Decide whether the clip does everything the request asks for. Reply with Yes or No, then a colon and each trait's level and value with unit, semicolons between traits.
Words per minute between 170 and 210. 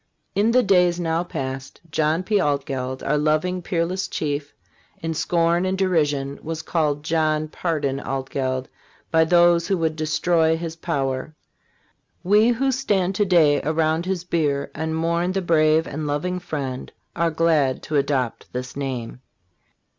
No: average, 145 wpm